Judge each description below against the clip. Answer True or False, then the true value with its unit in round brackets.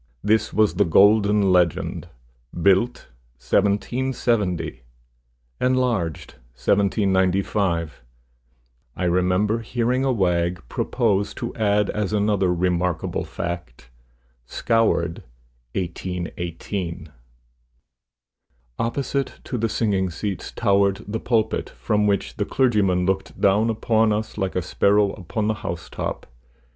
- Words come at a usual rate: False (105 wpm)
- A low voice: True (100 Hz)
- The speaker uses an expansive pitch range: False (3.3 semitones)